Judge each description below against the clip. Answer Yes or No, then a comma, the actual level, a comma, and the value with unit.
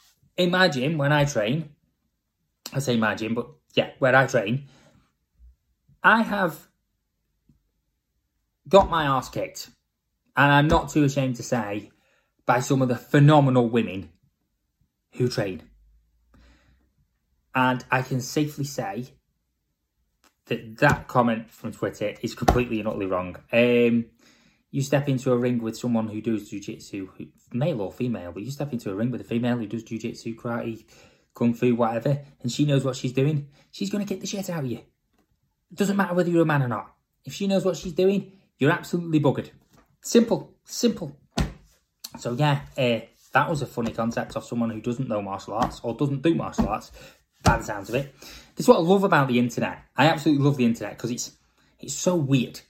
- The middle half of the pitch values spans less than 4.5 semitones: No, average, 4.8 semitones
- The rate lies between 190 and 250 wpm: No, average, 180 wpm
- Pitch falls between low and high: No, low, 125 Hz